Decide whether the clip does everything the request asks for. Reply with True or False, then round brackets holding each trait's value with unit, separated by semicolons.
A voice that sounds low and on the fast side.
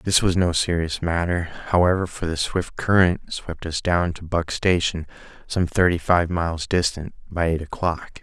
False (85 Hz; 175 wpm)